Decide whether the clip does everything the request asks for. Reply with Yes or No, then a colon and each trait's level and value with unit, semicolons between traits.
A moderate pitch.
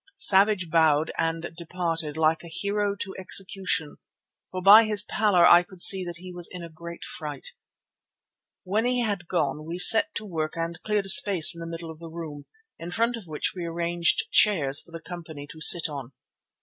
Yes: medium, 175 Hz